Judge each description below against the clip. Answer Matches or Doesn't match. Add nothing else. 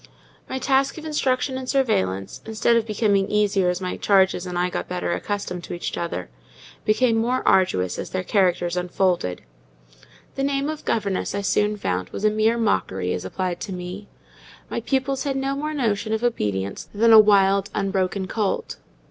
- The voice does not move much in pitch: Doesn't match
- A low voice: Doesn't match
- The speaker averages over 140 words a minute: Matches